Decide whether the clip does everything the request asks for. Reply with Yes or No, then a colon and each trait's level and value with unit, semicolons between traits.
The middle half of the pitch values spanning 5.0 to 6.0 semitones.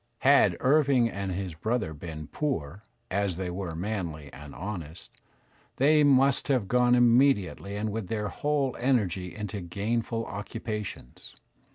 Yes: wide, 5.6 semitones